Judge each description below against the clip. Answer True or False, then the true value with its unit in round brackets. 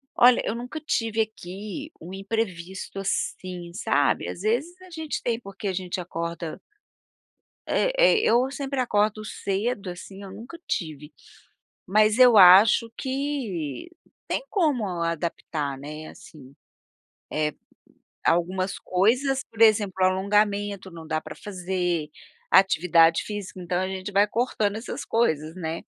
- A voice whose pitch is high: True (195 Hz)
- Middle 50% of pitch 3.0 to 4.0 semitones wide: False (4.7 semitones)